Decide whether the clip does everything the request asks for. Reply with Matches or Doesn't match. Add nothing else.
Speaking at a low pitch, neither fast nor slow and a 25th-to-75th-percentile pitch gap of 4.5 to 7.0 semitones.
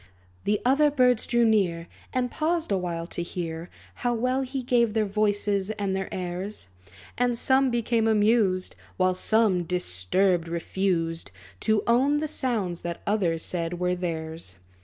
Doesn't match